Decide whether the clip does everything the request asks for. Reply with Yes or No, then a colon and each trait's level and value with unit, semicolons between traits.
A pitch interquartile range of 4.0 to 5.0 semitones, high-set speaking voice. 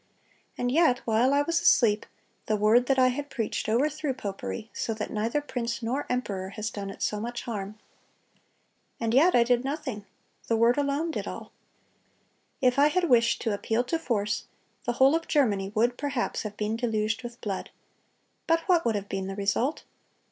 Yes: average, 4.5 semitones; high, 240 Hz